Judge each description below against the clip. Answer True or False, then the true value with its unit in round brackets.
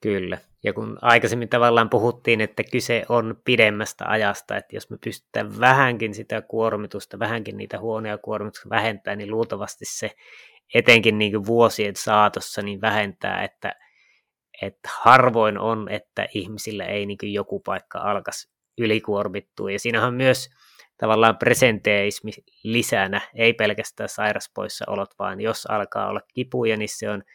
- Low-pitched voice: True (110 Hz)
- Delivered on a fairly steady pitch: True (1.9 semitones)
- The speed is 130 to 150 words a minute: True (145 wpm)